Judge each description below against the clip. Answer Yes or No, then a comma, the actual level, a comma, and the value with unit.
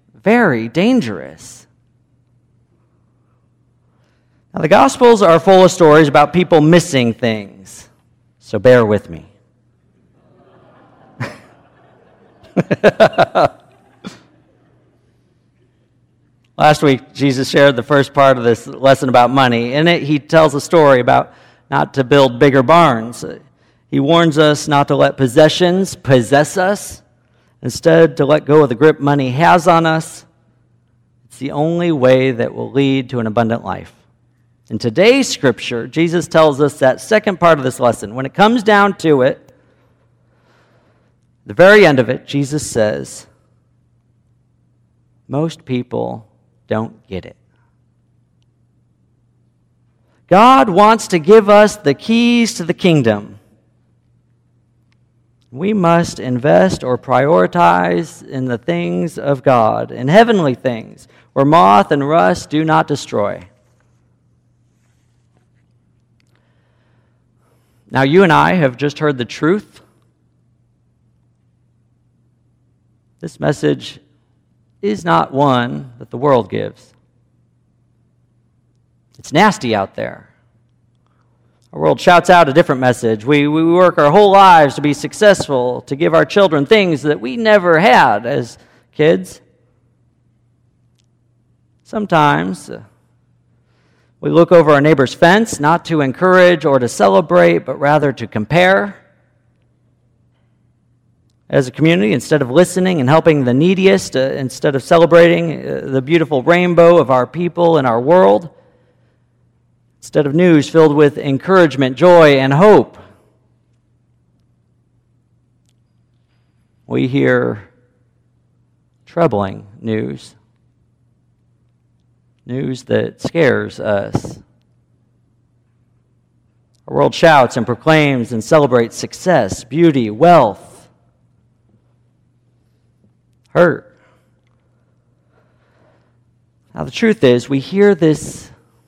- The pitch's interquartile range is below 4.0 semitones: No, average, 4.8 semitones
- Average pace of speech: No, slow, 110 wpm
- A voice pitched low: Yes, low, 125 Hz